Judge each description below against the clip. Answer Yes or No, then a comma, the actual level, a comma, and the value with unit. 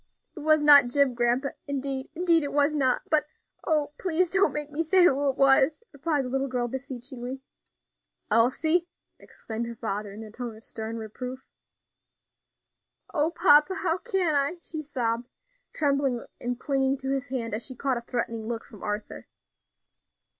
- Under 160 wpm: No, average, 165 wpm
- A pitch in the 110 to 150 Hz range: No, very high, 270 Hz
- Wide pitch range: No, average, 3.9 semitones